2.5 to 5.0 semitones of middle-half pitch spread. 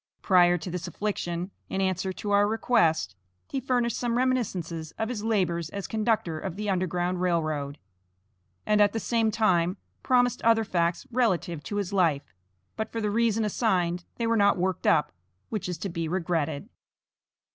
Yes: average, 4.4 semitones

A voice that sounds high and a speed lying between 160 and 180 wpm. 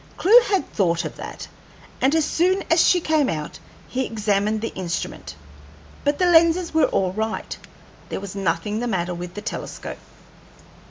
Yes: high, 220 Hz; average, 165 wpm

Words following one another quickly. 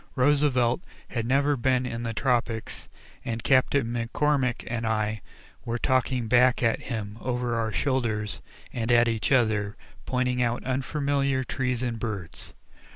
No: average, 140 wpm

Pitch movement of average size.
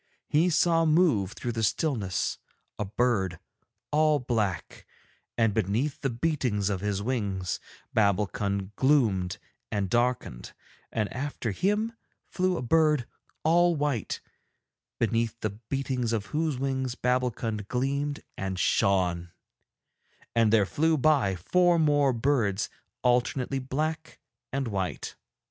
No: wide, 6.1 semitones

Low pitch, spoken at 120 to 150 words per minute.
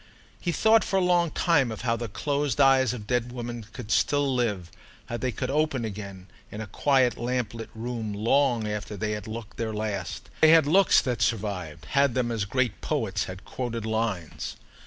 No: low, 115 Hz; average, 180 wpm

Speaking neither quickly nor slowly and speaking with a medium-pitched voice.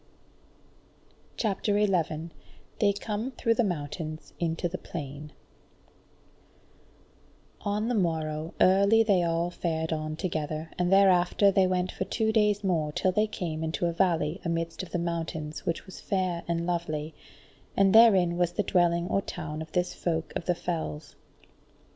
Yes: average, 150 wpm; medium, 175 Hz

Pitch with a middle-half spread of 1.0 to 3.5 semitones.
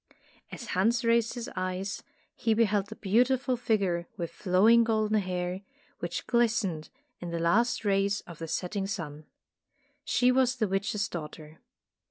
No: average, 4.3 semitones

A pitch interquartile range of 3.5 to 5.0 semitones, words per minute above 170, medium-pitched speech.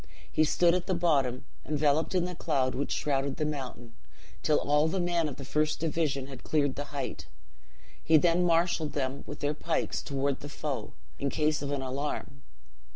No: average, 2.7 semitones; average, 185 wpm; medium, 150 Hz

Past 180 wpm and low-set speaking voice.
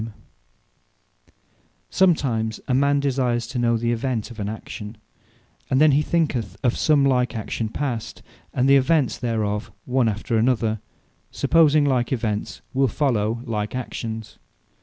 No: average, 140 wpm; low, 120 Hz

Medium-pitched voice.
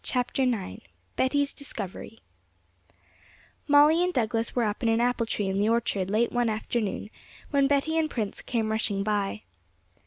No: high, 230 Hz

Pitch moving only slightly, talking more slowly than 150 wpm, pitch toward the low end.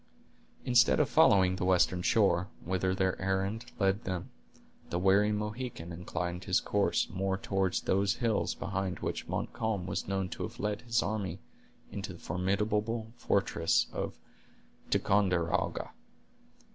Yes: narrow, 2.3 semitones; slow, 135 wpm; very low, 95 Hz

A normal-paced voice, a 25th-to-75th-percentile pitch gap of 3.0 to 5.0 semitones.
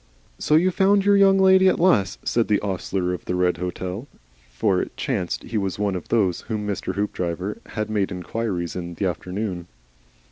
Yes: average, 185 wpm; average, 4.4 semitones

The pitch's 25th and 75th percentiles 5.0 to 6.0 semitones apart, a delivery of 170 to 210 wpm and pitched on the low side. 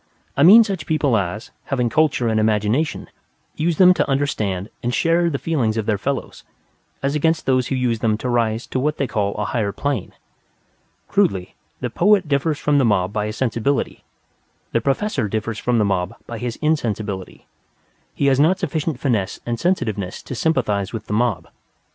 Yes: wide, 5.6 semitones; average, 180 wpm; low, 120 Hz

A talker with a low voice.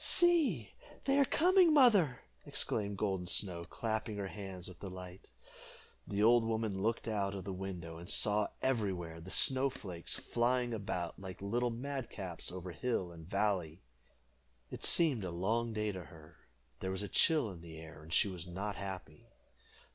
Yes: low, 100 Hz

